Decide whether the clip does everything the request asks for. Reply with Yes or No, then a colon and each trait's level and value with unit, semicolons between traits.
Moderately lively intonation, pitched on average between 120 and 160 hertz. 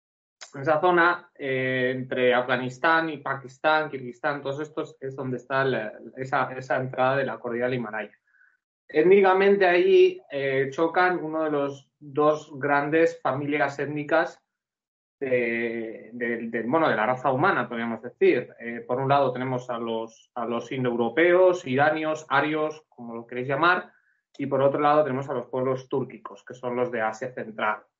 Yes: average, 3.7 semitones; low, 135 Hz